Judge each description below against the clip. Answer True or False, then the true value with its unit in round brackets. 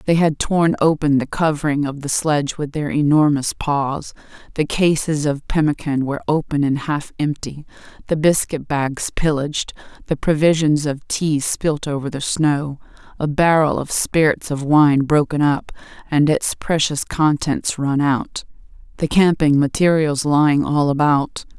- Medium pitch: True (150 Hz)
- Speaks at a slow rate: False (150 wpm)